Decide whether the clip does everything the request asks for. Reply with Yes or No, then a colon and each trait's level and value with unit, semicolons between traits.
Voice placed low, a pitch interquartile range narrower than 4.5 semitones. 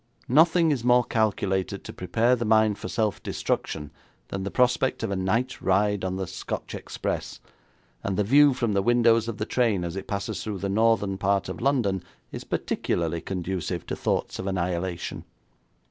Yes: low, 100 Hz; average, 3.8 semitones